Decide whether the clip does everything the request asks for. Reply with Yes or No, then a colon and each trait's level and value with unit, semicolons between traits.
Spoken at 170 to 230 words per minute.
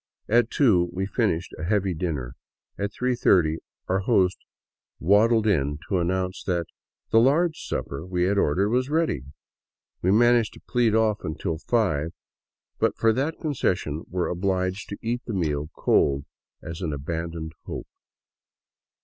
No: average, 150 wpm